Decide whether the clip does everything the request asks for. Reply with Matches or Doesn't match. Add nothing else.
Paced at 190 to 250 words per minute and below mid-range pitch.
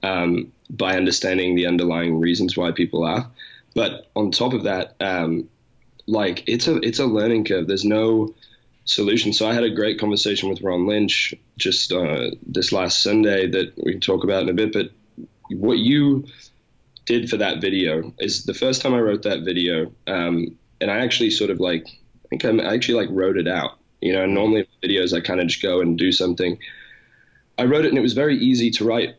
Matches